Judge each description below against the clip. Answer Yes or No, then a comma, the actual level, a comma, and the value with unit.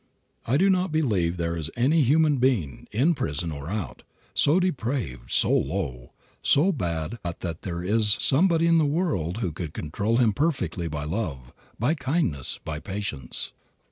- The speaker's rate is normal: Yes, average, 165 wpm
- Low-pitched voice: Yes, low, 105 Hz